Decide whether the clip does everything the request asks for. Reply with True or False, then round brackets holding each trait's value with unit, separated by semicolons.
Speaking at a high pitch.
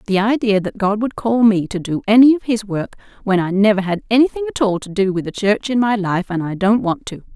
True (210 Hz)